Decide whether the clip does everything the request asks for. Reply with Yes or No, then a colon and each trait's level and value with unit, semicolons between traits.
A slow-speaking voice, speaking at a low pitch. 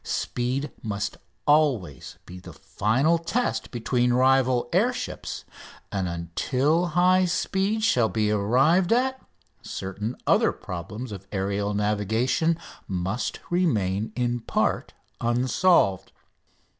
Yes: slow, 105 wpm; low, 120 Hz